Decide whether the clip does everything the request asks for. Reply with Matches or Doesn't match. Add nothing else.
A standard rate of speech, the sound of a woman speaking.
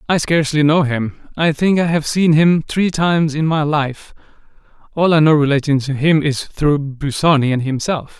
Doesn't match